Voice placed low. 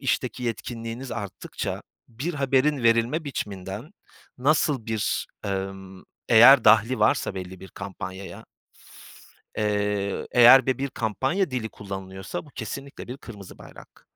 Yes: low, 115 Hz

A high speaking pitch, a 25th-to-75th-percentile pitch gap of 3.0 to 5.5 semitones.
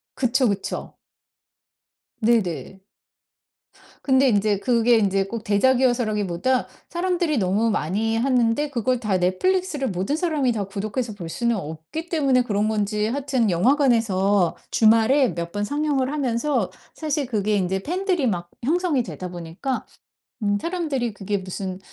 Yes: high, 230 Hz; average, 5.2 semitones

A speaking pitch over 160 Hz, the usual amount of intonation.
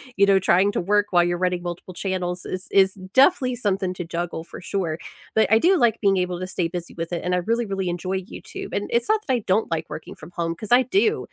Yes: high, 190 Hz; average, 3.6 semitones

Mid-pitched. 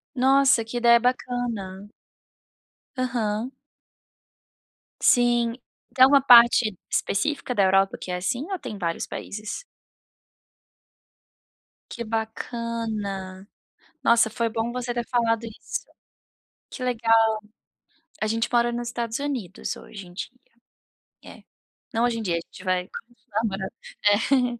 No: high, 230 Hz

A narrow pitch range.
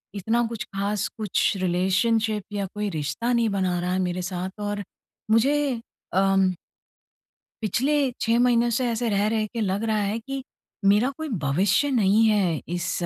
No: average, 3.4 semitones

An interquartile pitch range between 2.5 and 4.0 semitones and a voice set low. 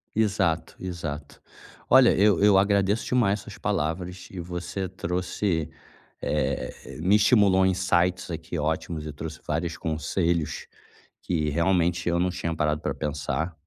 Yes: average, 2.9 semitones; very low, 90 Hz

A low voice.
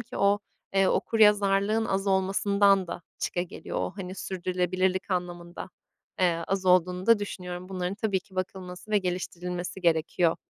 No: medium, 185 Hz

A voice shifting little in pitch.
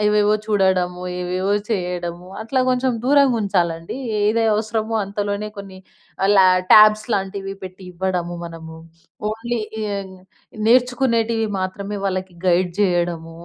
No: average, 3.4 semitones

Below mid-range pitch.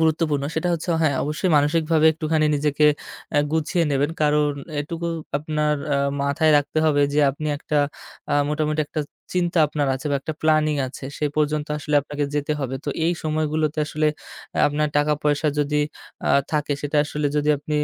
No: medium, 150 Hz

